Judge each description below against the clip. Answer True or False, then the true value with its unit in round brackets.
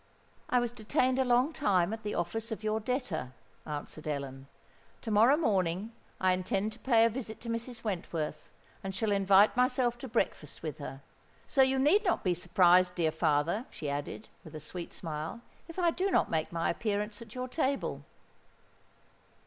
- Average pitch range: False (6.4 semitones)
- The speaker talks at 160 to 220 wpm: True (180 wpm)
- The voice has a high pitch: True (210 Hz)